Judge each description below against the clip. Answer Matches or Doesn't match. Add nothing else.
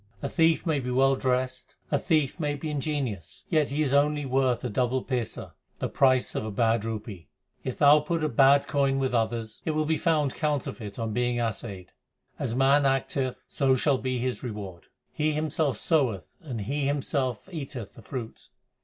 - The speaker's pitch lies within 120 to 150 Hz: Matches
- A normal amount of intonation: Matches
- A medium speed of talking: Matches